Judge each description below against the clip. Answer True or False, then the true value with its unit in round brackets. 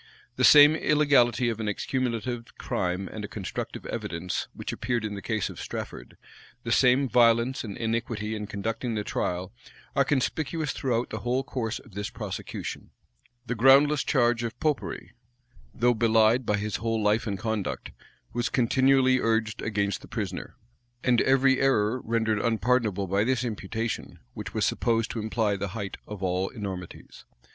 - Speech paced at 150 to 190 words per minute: True (160 wpm)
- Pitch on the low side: True (115 Hz)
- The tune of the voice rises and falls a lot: False (3.3 semitones)